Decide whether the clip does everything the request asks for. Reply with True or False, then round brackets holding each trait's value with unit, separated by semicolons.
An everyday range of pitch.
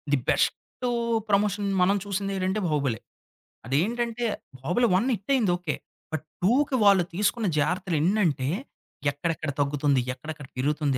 False (5.9 semitones)